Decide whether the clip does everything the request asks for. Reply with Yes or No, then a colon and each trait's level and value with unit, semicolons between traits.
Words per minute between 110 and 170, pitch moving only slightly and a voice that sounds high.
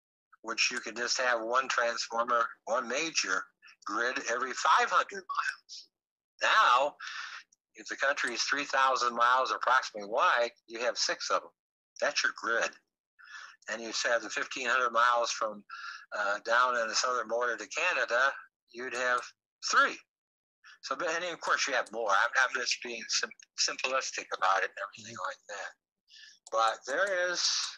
No: average, 150 wpm; narrow, 2.2 semitones; low, 120 Hz